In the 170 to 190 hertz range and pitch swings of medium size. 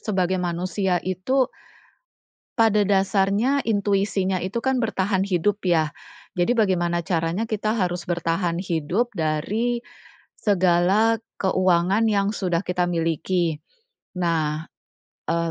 Yes: medium, 185 Hz; average, 3.2 semitones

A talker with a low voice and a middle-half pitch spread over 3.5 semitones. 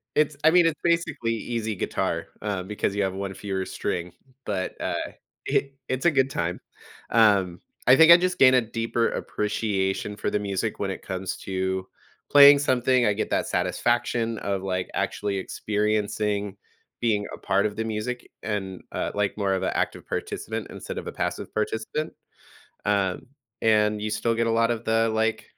No: low, 105 Hz; average, 3.2 semitones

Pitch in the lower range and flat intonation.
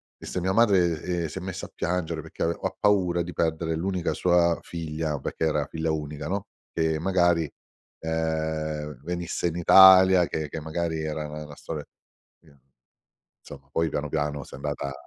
Yes: very low, 80 Hz; narrow, 2.3 semitones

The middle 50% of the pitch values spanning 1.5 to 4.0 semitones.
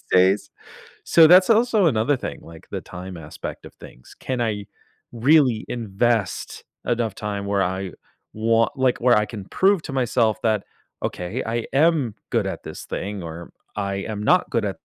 No: average, 4.8 semitones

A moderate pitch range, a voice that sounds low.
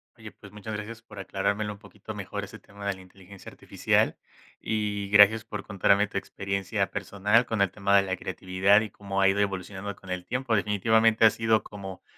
No: narrow, 1.5 semitones; low, 100 Hz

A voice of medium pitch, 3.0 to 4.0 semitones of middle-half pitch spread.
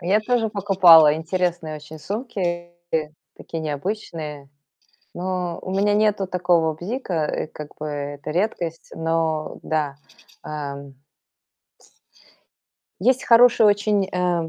No: medium, 175 Hz; average, 4.6 semitones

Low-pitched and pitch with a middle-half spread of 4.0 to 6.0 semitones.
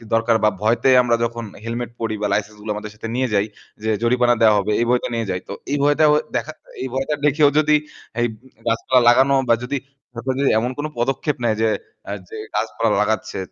No: low, 120 Hz; average, 3.1 semitones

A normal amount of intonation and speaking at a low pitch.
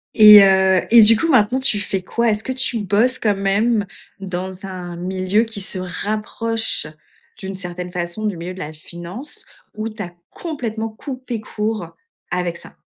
No: average, 3.5 semitones; high, 205 Hz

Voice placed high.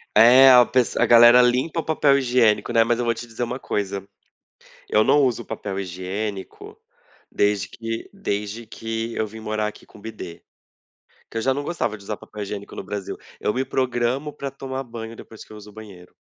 No: low, 115 Hz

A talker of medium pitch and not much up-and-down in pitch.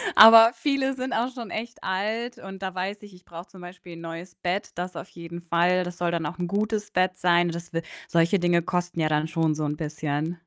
No: medium, 180 Hz; average, 3.2 semitones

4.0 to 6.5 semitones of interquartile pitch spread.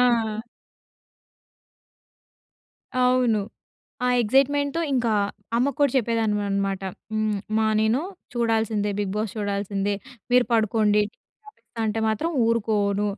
No: average, 3.0 semitones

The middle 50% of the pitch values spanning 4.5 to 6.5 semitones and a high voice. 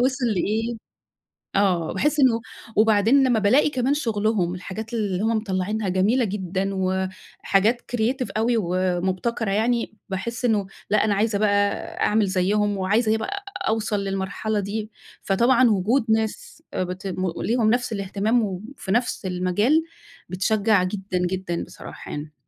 No: average, 3.4 semitones; high, 210 Hz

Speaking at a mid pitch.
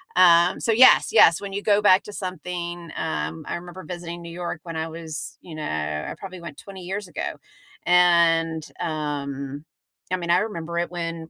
Yes: medium, 170 Hz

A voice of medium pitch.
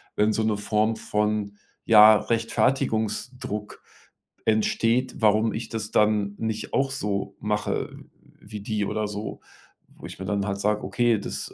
No: low, 105 Hz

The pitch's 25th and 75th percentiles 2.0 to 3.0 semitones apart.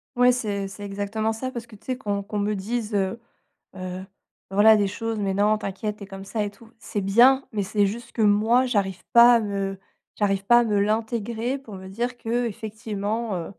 Yes: narrow, 2.6 semitones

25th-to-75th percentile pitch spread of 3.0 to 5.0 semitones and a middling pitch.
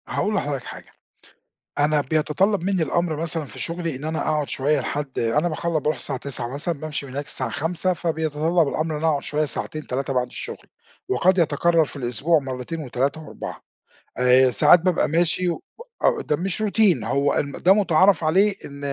Yes: average, 3.4 semitones; medium, 155 Hz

